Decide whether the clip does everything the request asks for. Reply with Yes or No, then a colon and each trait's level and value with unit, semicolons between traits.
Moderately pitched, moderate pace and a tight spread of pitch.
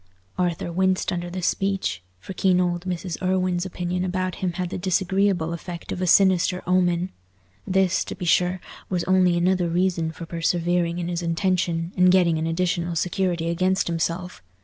Yes: medium, 180 Hz; average, 170 wpm; narrow, 1.4 semitones